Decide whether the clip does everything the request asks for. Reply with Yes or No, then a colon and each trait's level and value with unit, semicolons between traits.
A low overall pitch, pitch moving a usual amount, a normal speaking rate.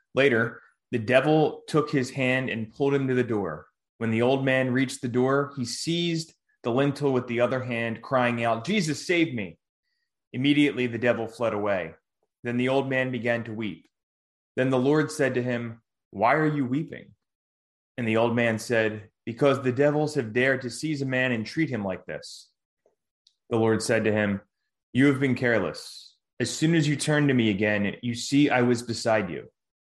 Yes: low, 125 Hz; average, 3.5 semitones; average, 190 wpm